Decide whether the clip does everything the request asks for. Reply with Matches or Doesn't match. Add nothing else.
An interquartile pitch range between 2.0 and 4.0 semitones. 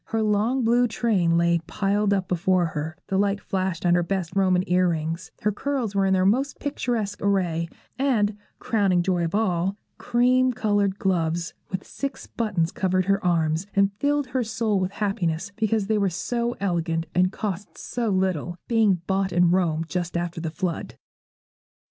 Matches